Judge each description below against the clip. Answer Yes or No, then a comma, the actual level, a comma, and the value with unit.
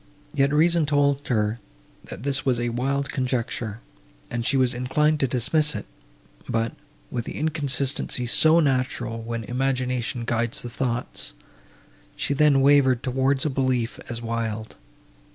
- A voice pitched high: No, low, 130 Hz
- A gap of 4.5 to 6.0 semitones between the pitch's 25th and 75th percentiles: No, average, 3.0 semitones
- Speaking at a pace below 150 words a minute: Yes, average, 140 wpm